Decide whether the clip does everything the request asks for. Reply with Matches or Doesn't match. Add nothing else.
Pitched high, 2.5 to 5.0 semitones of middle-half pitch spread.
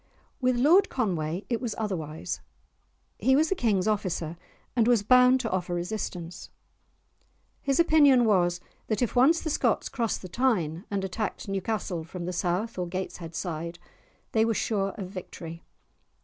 Doesn't match